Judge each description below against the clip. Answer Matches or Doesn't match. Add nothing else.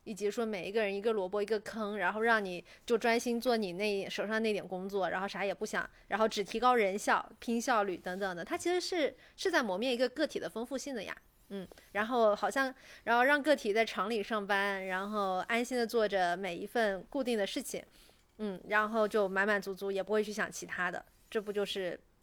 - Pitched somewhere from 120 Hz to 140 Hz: Doesn't match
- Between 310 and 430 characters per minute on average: Matches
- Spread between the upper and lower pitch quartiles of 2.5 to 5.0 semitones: Matches